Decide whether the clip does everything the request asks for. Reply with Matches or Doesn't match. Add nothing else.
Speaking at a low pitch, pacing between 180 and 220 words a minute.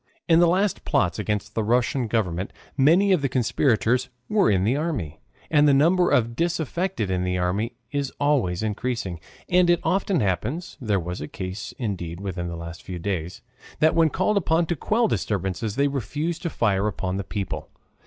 Matches